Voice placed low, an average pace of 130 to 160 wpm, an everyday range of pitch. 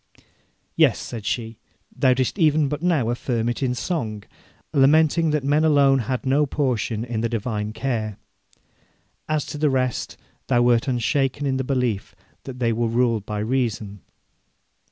Yes: low, 125 Hz; average, 155 wpm; average, 3.6 semitones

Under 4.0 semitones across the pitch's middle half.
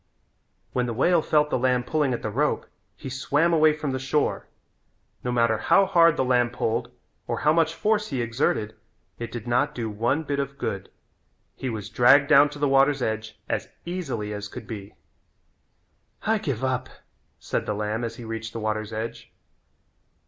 No: average, 4.7 semitones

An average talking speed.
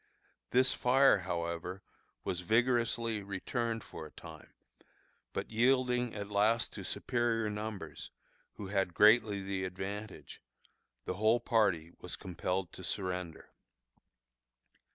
No: slow, 110 wpm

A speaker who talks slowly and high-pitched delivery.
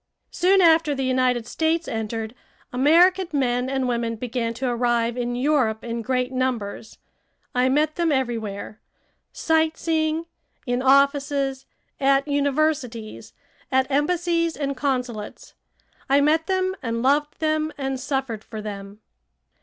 Yes: slow, 130 wpm; very high, 265 Hz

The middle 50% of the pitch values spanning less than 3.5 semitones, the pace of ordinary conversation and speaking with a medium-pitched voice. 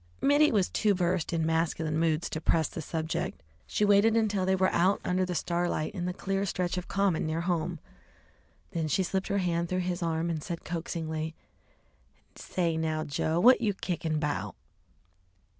Yes: average, 2.7 semitones; average, 175 wpm; medium, 175 Hz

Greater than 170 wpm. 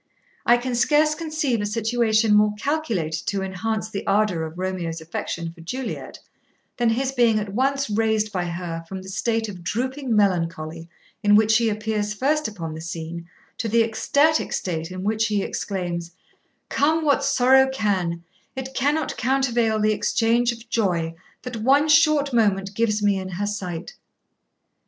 No: average, 160 wpm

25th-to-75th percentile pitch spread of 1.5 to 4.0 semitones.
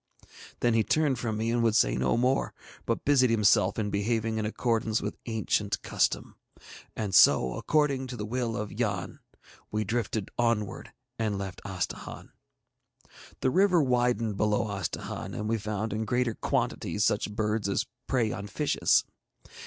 Yes: average, 2.7 semitones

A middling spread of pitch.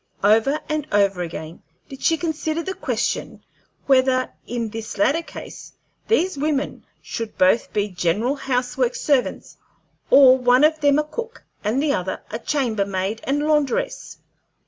No: wide, 5.7 semitones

